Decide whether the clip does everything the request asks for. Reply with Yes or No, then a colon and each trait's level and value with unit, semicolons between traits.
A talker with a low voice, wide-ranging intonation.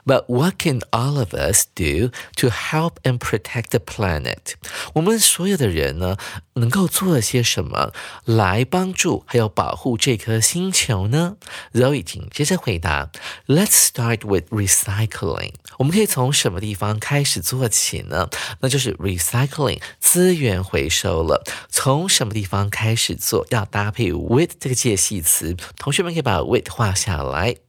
Yes: low, 120 Hz; wide, 5.8 semitones